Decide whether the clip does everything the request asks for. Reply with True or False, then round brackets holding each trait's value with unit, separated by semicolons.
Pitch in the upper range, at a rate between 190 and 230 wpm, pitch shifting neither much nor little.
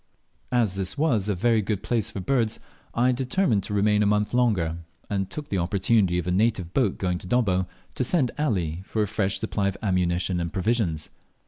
False (105 Hz; 200 wpm; 4.3 semitones)